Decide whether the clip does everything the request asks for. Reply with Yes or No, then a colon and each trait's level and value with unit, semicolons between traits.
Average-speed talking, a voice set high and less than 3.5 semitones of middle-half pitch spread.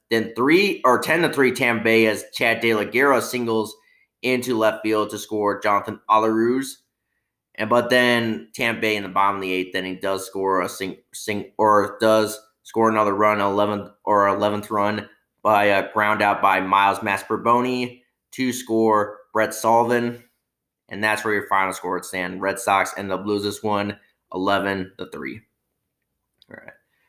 No: average, 175 wpm; low, 105 Hz; narrow, 2.5 semitones